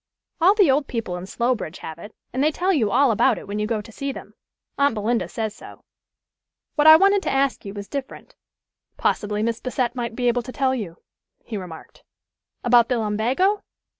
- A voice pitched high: Yes, high, 240 Hz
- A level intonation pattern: No, average, 4.7 semitones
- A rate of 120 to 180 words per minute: No, average, 200 wpm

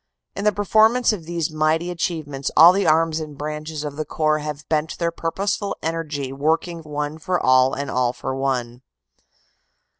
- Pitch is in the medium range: Yes, medium, 155 Hz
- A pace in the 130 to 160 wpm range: No, average, 170 wpm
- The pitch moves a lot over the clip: No, narrow, 2.6 semitones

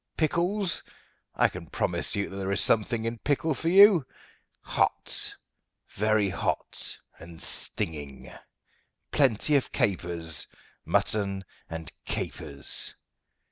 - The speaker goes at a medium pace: No, slow, 105 wpm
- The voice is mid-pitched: No, low, 105 Hz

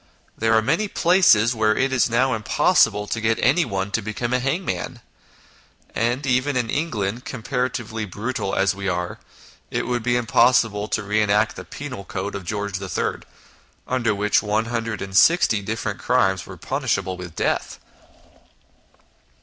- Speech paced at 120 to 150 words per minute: Yes, average, 140 wpm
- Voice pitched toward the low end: Yes, low, 110 Hz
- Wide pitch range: No, average, 3.6 semitones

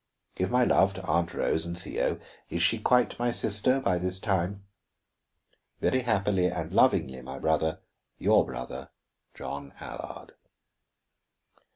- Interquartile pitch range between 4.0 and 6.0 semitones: Yes, average, 4.5 semitones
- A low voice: Yes, very low, 90 Hz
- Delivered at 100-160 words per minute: Yes, slow, 135 wpm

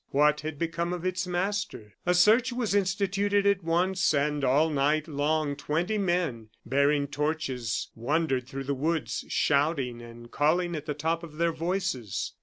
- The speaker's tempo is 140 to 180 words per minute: Yes, average, 160 wpm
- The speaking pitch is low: No, medium, 155 Hz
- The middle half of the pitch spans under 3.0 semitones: No, average, 4.1 semitones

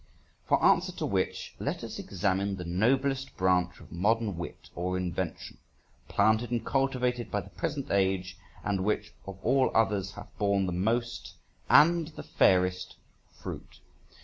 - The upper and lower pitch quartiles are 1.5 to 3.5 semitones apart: No, average, 4.7 semitones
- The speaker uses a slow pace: No, average, 150 wpm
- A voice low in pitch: Yes, low, 100 Hz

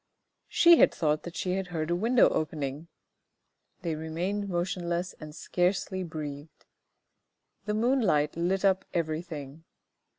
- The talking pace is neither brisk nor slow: No, slow, 125 wpm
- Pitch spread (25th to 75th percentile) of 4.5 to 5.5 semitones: No, average, 3.4 semitones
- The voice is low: No, medium, 175 Hz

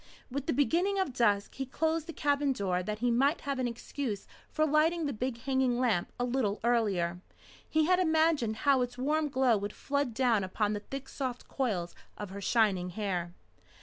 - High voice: Yes, very high, 250 Hz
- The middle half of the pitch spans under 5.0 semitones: No, average, 5.3 semitones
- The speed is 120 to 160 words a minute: No, average, 190 wpm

